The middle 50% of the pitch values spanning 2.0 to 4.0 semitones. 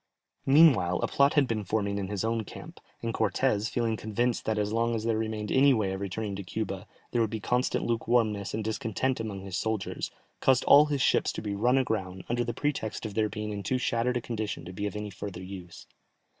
Yes: average, 2.9 semitones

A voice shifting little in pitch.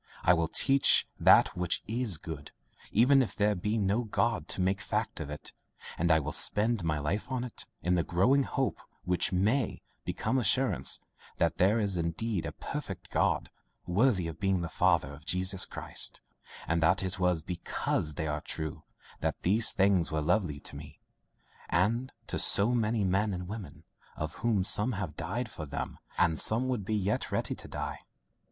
No: average, 5.0 semitones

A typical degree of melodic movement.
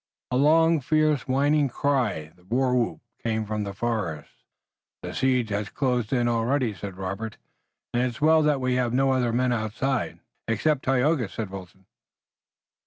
Yes: average, 4.0 semitones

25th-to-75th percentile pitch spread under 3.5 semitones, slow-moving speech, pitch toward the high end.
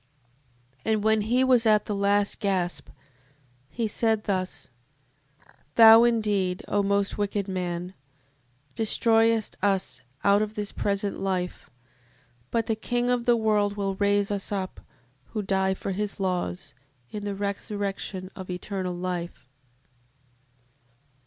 Yes: narrow, 2.4 semitones; slow, 125 wpm; high, 200 Hz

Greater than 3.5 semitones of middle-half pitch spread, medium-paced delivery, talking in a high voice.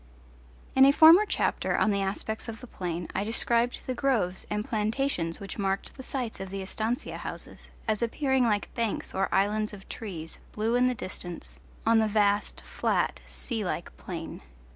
Yes: average, 3.9 semitones; average, 175 wpm; high, 215 Hz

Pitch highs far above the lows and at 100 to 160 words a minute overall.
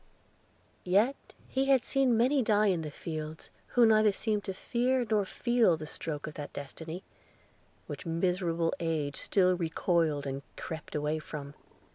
Yes: wide, 6.1 semitones; average, 150 wpm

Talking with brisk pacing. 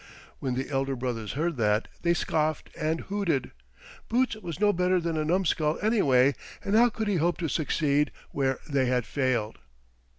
No: average, 170 wpm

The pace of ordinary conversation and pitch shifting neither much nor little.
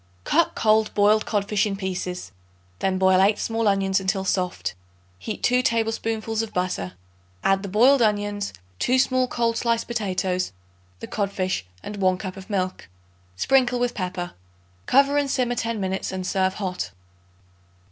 Yes: average, 150 wpm; average, 3.3 semitones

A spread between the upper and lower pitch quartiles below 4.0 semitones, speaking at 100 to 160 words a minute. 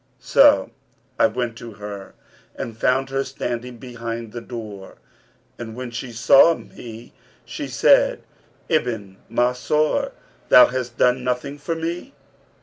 Yes: narrow, 2.6 semitones; slow, 135 wpm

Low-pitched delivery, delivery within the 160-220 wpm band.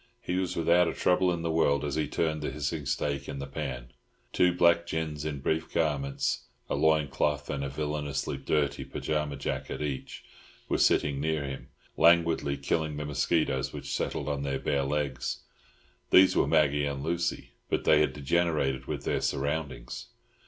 Yes: very low, 75 Hz; average, 165 wpm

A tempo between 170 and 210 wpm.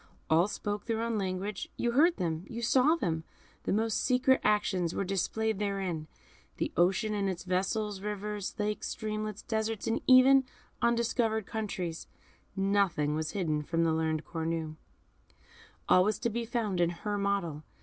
No: average, 155 wpm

